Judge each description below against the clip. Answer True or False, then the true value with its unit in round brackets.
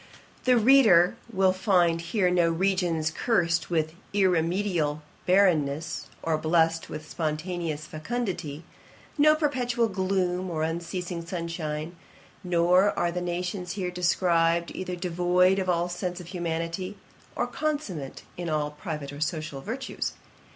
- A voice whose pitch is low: False (175 Hz)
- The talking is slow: True (125 wpm)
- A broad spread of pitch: False (2.5 semitones)